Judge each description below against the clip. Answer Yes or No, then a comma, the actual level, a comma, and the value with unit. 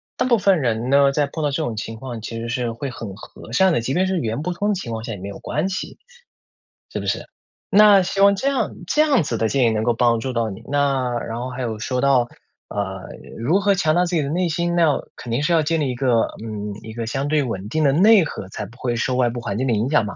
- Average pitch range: No, wide, 6.3 semitones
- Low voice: Yes, low, 130 Hz